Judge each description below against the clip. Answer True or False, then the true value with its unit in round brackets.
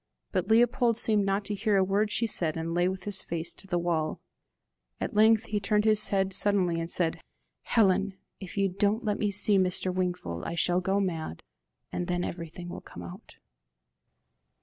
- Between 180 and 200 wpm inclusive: True (190 wpm)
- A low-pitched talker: False (190 Hz)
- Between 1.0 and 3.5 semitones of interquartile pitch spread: True (3.0 semitones)